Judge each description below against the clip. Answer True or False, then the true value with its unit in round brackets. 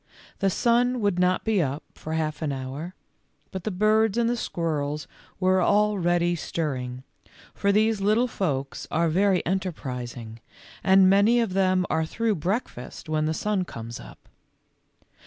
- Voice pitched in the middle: True (180 Hz)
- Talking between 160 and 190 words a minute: False (150 wpm)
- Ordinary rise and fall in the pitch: True (5.0 semitones)